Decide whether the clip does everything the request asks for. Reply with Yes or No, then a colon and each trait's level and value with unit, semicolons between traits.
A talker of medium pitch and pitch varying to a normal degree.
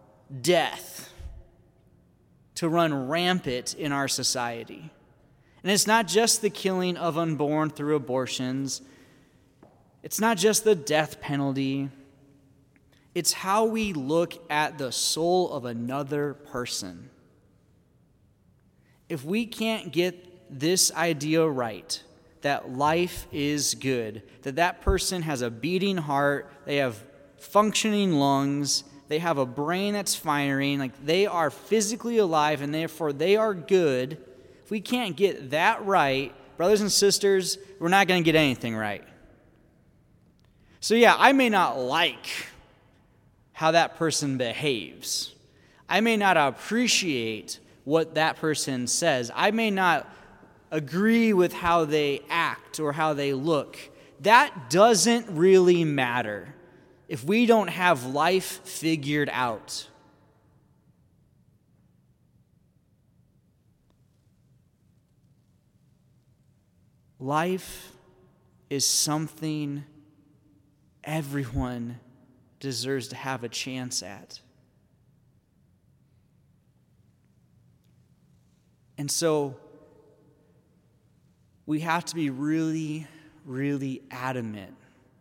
Yes: medium, 150 Hz; average, 4.8 semitones